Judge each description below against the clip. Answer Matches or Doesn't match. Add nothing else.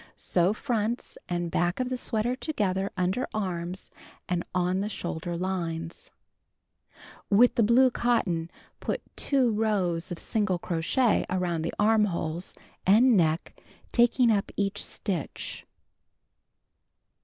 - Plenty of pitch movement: Doesn't match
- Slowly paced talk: Matches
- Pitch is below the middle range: Doesn't match